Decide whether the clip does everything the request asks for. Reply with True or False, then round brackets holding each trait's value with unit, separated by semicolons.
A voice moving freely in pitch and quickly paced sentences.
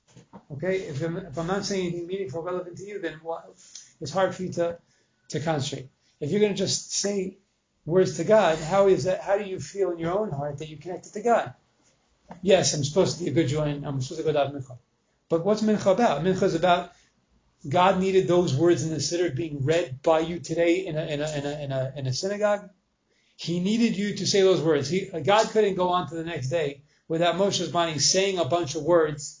False (3.8 semitones; 230 wpm)